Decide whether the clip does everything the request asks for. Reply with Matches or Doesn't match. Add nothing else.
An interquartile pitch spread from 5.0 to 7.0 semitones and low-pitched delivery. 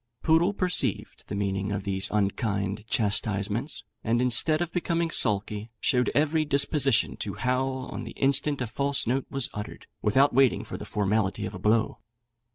Matches